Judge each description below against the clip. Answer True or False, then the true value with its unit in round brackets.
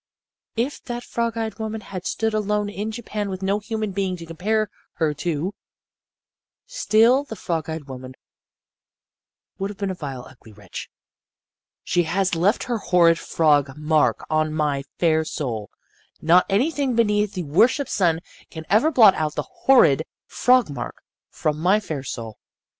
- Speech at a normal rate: True (155 wpm)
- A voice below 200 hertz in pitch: True (185 Hz)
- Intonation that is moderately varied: False (5.8 semitones)